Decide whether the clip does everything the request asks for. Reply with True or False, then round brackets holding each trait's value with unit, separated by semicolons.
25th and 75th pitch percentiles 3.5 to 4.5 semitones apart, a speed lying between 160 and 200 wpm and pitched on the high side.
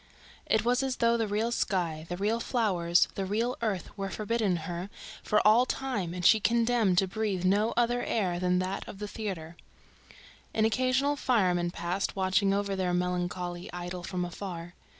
True (4.1 semitones; 170 wpm; 195 Hz)